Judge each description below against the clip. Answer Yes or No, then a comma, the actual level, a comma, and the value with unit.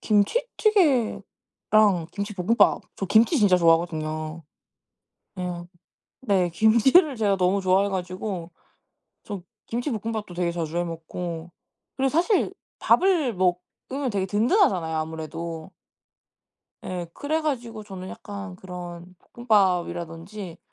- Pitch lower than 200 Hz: Yes, high, 190 Hz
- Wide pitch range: No, average, 4.6 semitones